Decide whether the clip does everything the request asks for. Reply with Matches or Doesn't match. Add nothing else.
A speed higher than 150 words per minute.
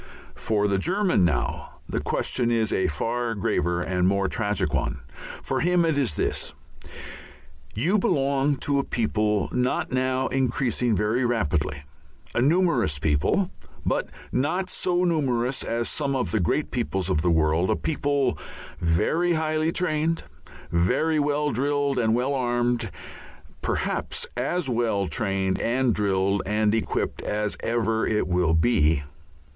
Doesn't match